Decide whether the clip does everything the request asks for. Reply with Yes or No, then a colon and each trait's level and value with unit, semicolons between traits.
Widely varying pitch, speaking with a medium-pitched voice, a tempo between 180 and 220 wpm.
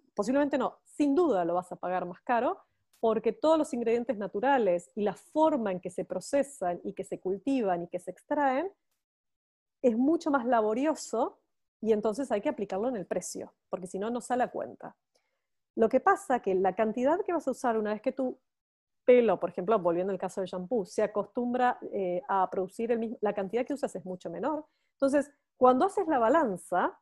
No: wide, 6.5 semitones; high, 230 Hz; average, 200 wpm